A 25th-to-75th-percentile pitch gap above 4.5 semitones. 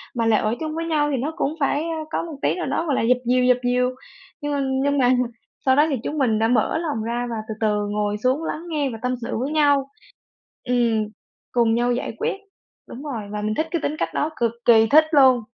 No: average, 4.2 semitones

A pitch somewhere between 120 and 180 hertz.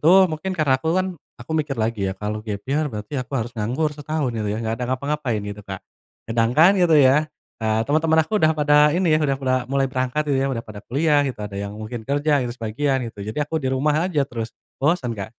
Yes: low, 135 Hz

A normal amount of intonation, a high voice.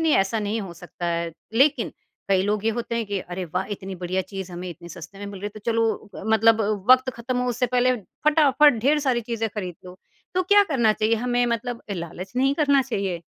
Yes: average, 4.8 semitones; high, 220 Hz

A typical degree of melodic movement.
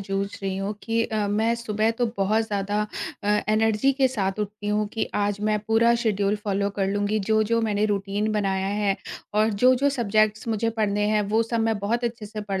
No: narrow, 1.7 semitones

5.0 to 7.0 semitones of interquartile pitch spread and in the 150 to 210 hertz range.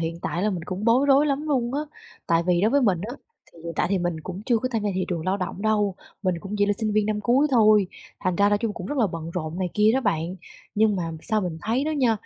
No: average, 4.4 semitones; high, 205 Hz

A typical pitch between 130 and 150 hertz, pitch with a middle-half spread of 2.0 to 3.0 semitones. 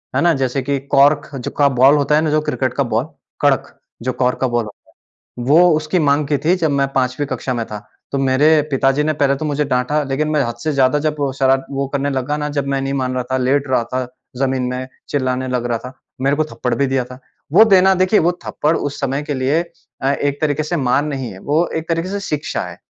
Yes: medium, 140 Hz; narrow, 2.6 semitones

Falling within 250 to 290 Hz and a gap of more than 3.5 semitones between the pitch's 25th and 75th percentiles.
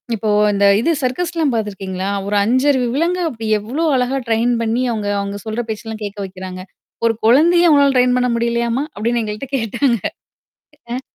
No: high, 235 Hz; average, 4.1 semitones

